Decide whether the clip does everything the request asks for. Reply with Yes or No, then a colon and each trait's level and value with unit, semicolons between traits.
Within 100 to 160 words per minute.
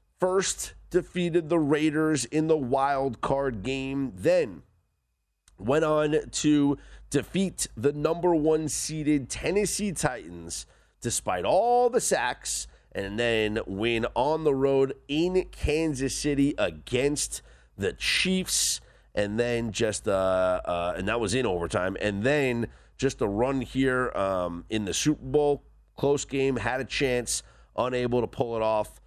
Yes: average, 140 wpm